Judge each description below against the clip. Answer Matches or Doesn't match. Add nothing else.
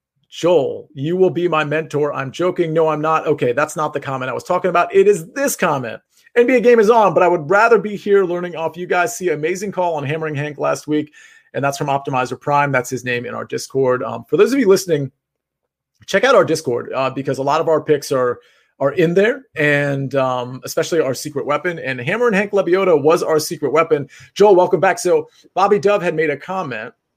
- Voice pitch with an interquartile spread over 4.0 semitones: Matches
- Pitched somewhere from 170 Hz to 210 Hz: Doesn't match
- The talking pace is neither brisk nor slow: Doesn't match